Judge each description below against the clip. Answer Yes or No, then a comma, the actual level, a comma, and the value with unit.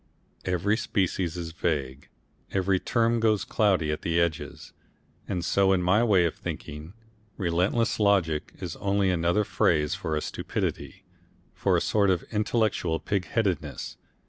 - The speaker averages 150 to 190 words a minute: No, average, 140 wpm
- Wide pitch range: No, average, 3.6 semitones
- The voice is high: No, very low, 95 Hz